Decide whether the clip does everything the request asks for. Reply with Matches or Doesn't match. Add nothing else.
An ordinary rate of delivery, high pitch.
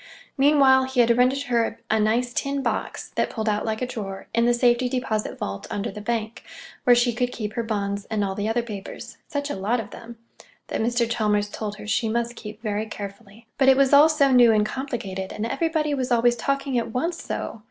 Doesn't match